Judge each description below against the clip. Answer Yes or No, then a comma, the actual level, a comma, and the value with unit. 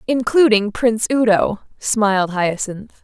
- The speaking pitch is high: Yes, high, 220 Hz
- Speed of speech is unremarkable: No, slow, 100 wpm